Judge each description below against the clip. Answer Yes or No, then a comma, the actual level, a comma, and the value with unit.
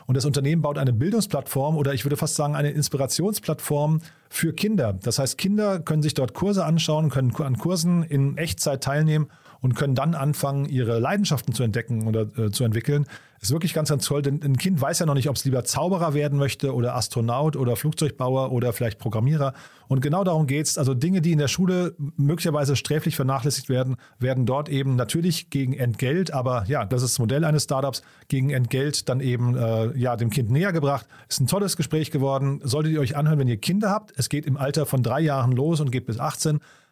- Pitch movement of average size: Yes, average, 3.1 semitones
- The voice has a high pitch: No, medium, 140 Hz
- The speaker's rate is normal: No, fast, 210 wpm